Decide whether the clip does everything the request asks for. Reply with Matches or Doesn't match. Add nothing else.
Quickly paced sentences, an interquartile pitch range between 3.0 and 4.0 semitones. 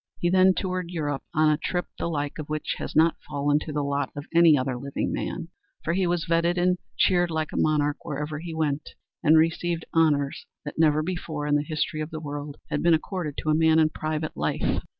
Doesn't match